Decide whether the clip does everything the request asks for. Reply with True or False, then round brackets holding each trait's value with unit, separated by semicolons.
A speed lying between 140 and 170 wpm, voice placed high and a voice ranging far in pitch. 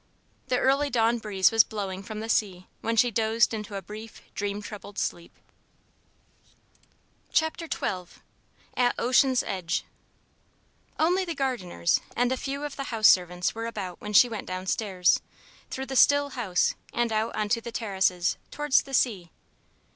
False (155 wpm; 225 Hz; 4.6 semitones)